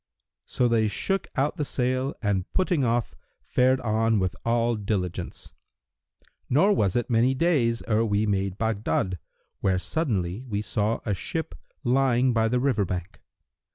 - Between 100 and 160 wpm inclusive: Yes, average, 150 wpm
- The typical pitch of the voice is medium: No, low, 115 Hz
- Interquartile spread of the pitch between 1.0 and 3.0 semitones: No, average, 4.0 semitones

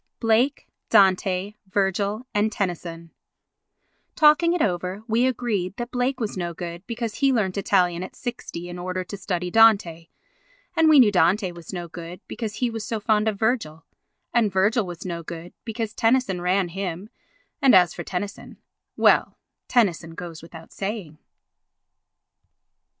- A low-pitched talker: No, high, 195 Hz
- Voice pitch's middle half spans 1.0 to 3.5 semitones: No, average, 4.3 semitones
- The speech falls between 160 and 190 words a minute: No, average, 150 wpm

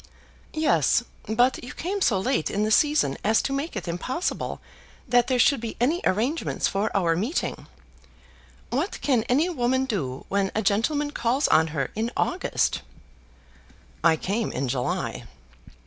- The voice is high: Yes, high, 235 Hz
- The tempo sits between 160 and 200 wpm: No, average, 150 wpm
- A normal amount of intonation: No, wide, 6.1 semitones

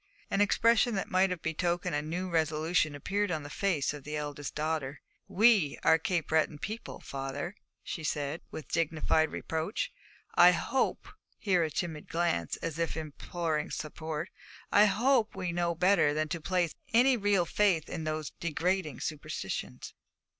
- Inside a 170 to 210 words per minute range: No, average, 160 wpm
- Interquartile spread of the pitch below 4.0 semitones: Yes, average, 3.5 semitones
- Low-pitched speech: No, medium, 165 Hz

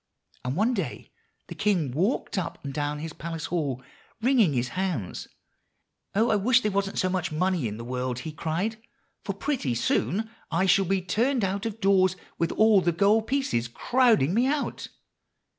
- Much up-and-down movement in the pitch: Yes, wide, 6.0 semitones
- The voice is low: No, medium, 185 Hz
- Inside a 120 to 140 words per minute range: No, average, 175 wpm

